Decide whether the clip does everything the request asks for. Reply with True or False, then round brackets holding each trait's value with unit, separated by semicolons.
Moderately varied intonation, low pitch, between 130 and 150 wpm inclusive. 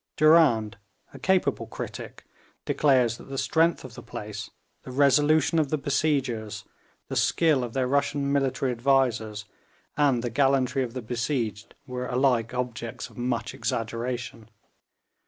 True (3.2 semitones; 130 Hz; 135 wpm)